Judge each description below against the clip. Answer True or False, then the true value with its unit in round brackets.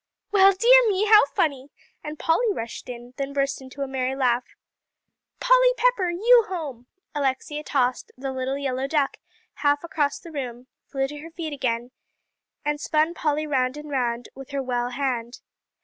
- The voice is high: True (280 Hz)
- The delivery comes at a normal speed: True (165 wpm)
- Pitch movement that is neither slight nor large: True (4.1 semitones)